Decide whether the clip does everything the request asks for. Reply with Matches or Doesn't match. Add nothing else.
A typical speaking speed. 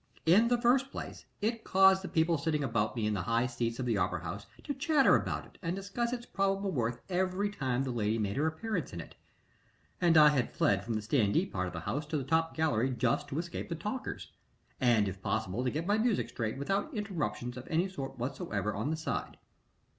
Doesn't match